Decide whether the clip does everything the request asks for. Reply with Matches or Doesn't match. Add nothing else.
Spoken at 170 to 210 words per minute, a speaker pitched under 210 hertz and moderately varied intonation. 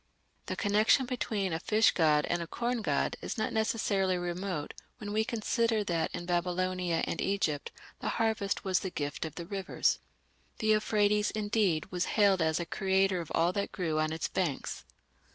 Matches